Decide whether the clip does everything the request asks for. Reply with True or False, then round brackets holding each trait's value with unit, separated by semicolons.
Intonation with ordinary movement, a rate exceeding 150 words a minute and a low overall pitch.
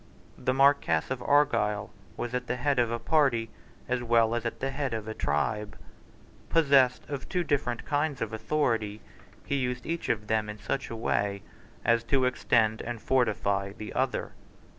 True (3.8 semitones; 165 wpm; 120 Hz)